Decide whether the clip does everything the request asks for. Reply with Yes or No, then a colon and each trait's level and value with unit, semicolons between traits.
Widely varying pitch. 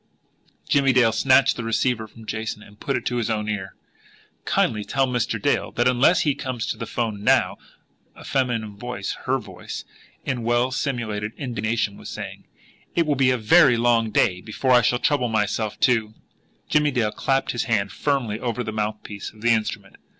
No: average, 2.9 semitones